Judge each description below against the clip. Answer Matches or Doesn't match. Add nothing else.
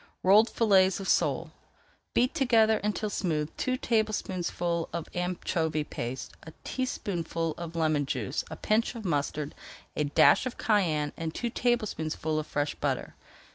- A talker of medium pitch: Matches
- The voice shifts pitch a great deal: Matches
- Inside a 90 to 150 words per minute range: Matches